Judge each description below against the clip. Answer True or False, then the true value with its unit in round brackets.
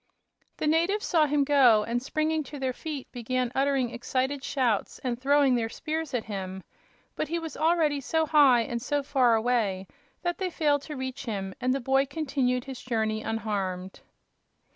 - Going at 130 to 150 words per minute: False (175 wpm)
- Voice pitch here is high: True (265 Hz)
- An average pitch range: True (4.0 semitones)